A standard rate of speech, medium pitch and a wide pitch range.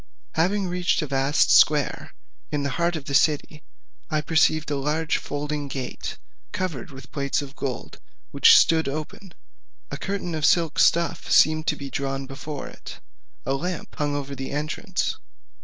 No: average, 160 wpm; medium, 150 Hz; narrow, 2.6 semitones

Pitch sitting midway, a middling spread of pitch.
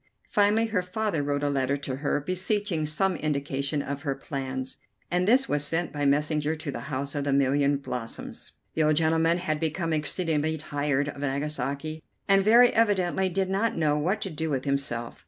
Yes: medium, 150 Hz; average, 4.2 semitones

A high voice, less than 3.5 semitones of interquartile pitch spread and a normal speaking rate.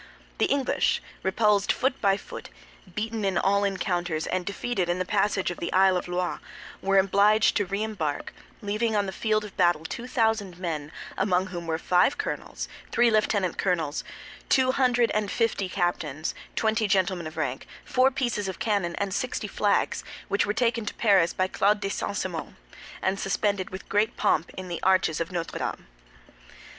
Yes: high, 195 Hz; average, 3.1 semitones; average, 175 wpm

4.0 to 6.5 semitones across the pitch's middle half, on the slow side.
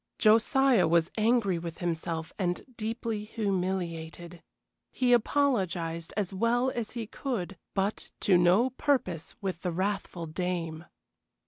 Yes: average, 5.1 semitones; slow, 120 wpm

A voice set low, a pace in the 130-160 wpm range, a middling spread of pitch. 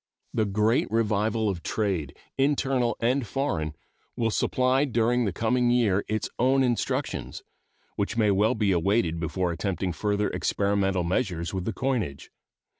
Yes: low, 105 Hz; average, 140 wpm; average, 4.1 semitones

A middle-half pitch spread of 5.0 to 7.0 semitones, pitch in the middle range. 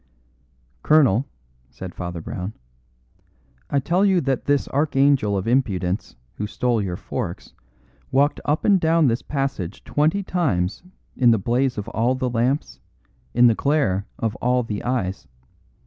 No: wide, 5.6 semitones; low, 125 Hz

